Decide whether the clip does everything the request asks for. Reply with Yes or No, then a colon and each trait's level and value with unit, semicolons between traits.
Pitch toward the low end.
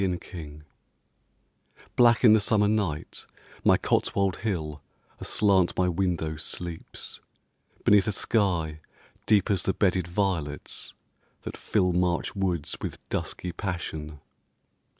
Yes: very low, 90 Hz